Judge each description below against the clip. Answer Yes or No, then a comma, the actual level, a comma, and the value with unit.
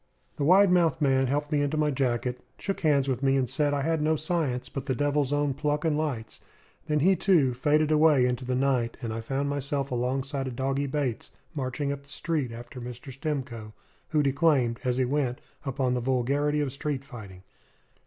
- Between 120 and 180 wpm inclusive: No, average, 200 wpm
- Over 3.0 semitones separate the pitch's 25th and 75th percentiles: No, average, 2.7 semitones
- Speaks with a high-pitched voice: No, medium, 140 Hz